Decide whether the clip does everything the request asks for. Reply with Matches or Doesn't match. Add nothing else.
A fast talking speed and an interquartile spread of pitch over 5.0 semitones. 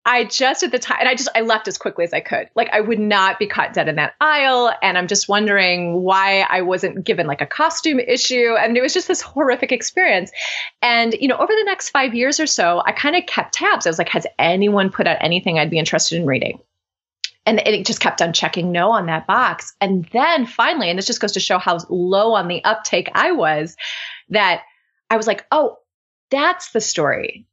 Matches